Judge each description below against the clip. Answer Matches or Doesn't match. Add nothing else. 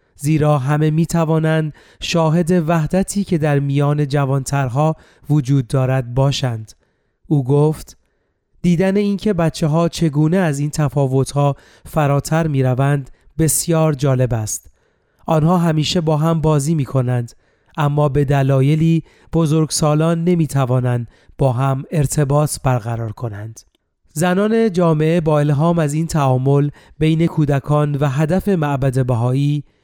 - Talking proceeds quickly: Doesn't match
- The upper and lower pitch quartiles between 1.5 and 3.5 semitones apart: Matches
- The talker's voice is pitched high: Doesn't match